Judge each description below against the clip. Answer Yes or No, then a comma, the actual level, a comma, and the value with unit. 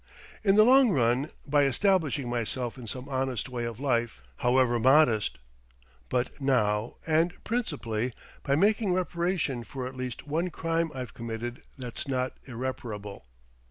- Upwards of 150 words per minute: No, average, 140 wpm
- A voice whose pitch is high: No, low, 130 Hz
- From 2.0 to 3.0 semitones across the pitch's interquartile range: No, average, 4.9 semitones